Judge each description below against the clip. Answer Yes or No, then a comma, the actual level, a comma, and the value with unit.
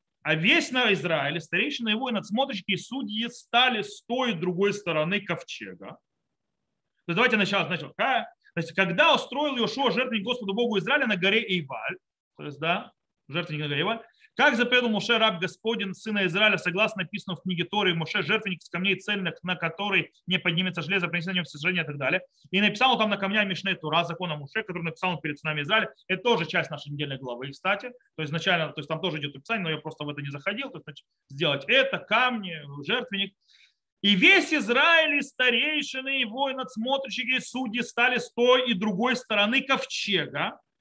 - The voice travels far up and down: Yes, wide, 6.0 semitones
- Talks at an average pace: No, fast, 190 wpm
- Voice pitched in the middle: No, high, 200 Hz